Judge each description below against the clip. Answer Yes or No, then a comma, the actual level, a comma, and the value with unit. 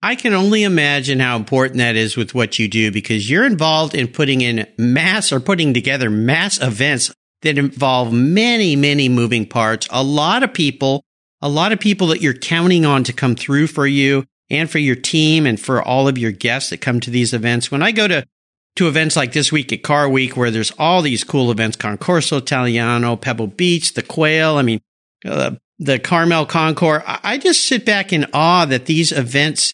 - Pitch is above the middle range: No, medium, 140 Hz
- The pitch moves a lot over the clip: No, average, 4.8 semitones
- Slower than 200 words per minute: No, fast, 205 wpm